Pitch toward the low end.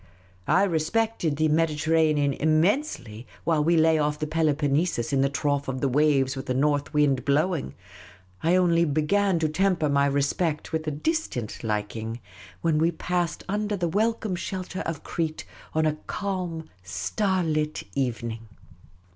No: medium, 155 Hz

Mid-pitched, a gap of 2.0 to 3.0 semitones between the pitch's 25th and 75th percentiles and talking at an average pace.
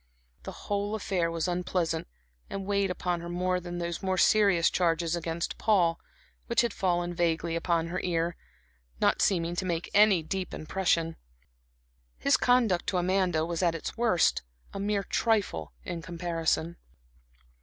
Yes: medium, 175 Hz; narrow, 2.4 semitones; average, 150 wpm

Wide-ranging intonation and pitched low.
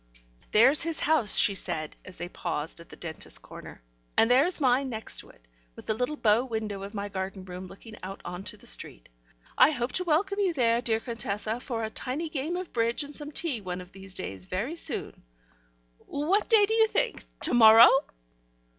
No: wide, 7.4 semitones; high, 230 Hz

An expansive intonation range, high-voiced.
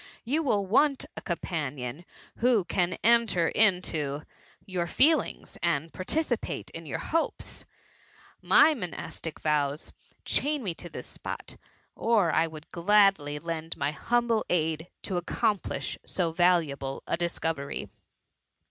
No: wide, 5.7 semitones; medium, 175 Hz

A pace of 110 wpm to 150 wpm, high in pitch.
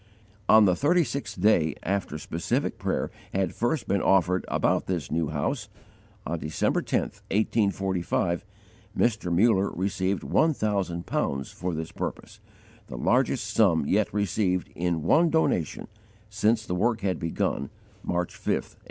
No: average, 145 wpm; very low, 95 Hz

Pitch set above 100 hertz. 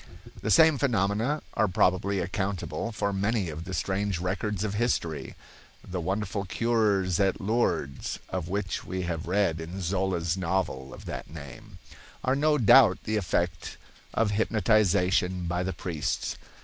No: very low, 95 Hz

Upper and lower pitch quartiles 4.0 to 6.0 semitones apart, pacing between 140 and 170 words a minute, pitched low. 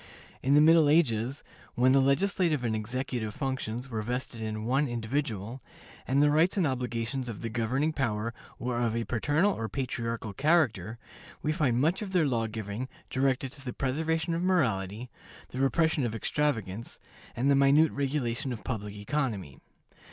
Yes: average, 4.4 semitones; average, 165 wpm; low, 130 Hz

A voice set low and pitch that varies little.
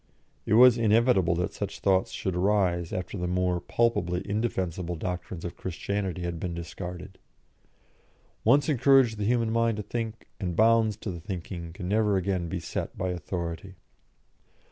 No: very low, 95 Hz; average, 3.8 semitones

